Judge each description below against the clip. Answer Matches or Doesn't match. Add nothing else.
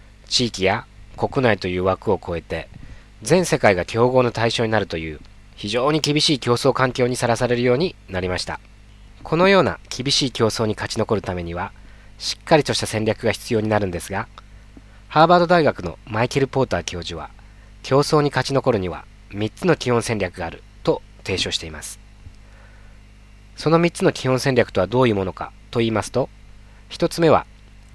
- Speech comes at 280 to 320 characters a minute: Doesn't match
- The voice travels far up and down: Doesn't match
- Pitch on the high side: Doesn't match